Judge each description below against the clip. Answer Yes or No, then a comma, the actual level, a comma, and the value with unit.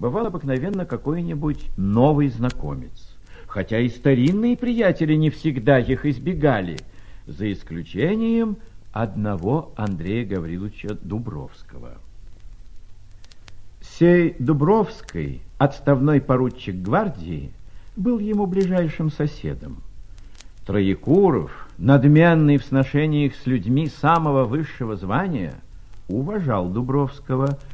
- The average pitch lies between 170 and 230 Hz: No, low, 130 Hz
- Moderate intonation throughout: No, wide, 7.2 semitones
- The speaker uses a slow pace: Yes, slow, 85 wpm